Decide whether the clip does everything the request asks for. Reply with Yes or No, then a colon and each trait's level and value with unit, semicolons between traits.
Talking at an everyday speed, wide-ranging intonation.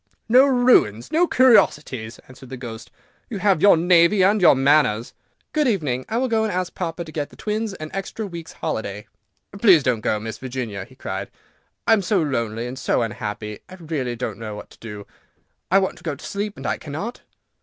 No: fast, 210 wpm; wide, 9.0 semitones